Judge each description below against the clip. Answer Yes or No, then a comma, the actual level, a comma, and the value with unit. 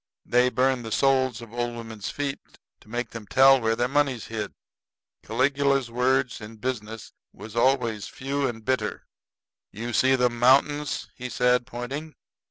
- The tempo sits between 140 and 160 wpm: Yes, average, 155 wpm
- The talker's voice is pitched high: No, low, 125 Hz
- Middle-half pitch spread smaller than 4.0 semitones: Yes, narrow, 2.6 semitones